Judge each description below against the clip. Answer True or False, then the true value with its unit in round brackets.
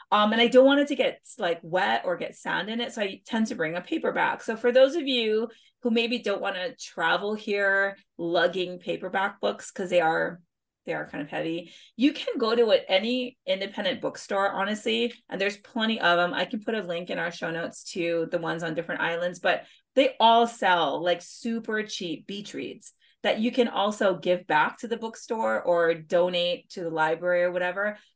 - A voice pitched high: True (200 Hz)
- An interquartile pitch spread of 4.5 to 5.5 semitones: True (5.0 semitones)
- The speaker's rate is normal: False (210 wpm)